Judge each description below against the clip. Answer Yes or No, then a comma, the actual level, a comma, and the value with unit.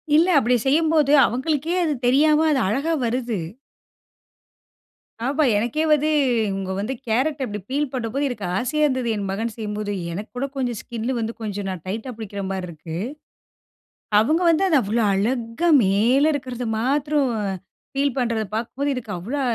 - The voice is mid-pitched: No, high, 245 Hz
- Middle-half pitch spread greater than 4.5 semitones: Yes, average, 5.0 semitones